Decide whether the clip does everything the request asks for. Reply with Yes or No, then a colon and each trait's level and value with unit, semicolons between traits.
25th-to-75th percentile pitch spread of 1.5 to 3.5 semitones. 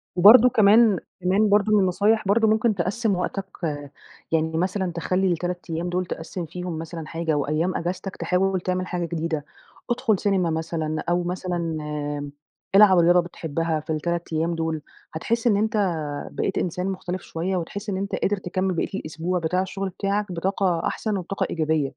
Yes: average, 3.0 semitones